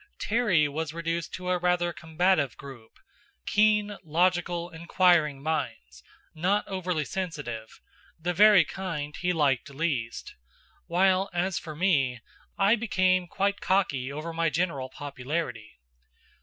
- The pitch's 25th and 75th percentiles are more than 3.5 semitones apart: Yes, average, 4.2 semitones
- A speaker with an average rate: No, slow, 120 wpm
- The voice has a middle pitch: Yes, medium, 170 Hz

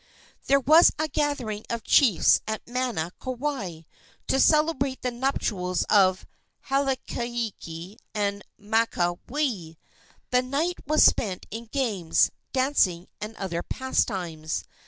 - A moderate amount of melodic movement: No, wide, 6.3 semitones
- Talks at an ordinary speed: No, slow, 110 wpm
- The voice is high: Yes, high, 230 Hz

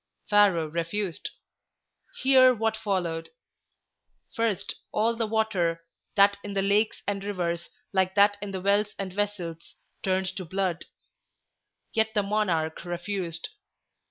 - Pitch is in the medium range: No, high, 200 Hz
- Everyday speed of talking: No, slow, 125 wpm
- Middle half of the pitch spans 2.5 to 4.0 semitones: Yes, average, 3.2 semitones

